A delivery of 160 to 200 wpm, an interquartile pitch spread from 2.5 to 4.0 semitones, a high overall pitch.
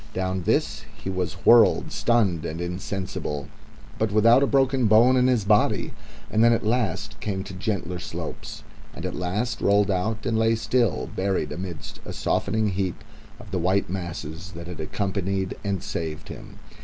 No: average, 165 wpm; average, 3.6 semitones; very low, 95 Hz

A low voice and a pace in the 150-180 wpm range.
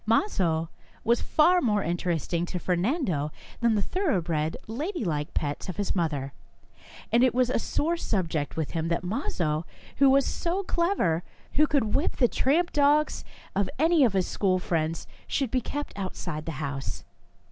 No: high, 200 Hz; average, 160 wpm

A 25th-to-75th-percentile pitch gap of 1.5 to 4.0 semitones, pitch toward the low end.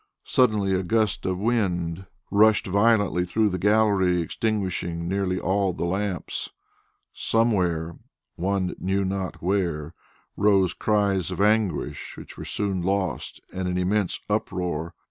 Yes: narrow, 2.5 semitones; very low, 95 Hz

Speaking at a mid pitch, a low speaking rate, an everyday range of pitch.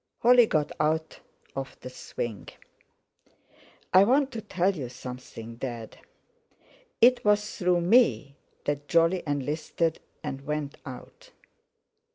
No: medium, 155 Hz; slow, 115 wpm; wide, 6.7 semitones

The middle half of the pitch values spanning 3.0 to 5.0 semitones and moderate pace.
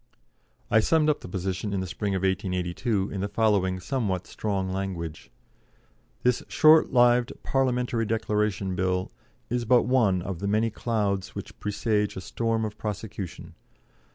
Yes: average, 3.4 semitones; average, 150 wpm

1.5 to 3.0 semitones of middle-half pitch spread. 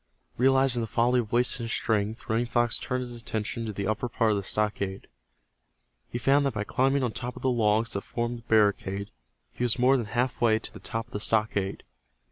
Yes: narrow, 2.5 semitones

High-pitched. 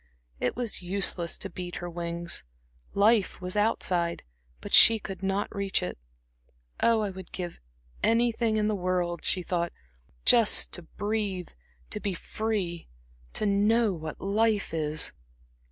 Yes: high, 195 Hz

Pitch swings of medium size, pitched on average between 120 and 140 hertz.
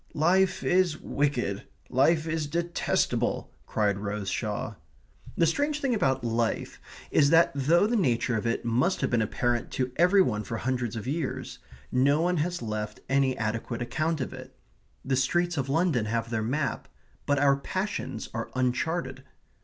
No: wide, 6.1 semitones; low, 135 Hz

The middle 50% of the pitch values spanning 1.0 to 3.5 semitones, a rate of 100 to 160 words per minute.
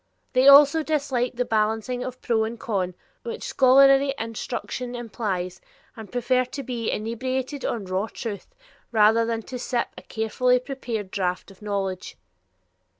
Yes: average, 3.2 semitones; average, 145 wpm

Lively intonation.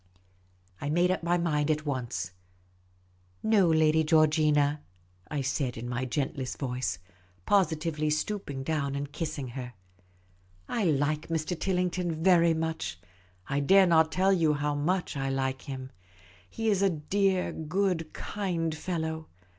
No: average, 4.2 semitones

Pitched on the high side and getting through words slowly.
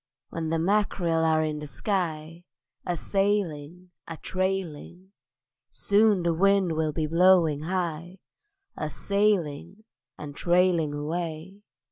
No: medium, 170 Hz; slow, 115 wpm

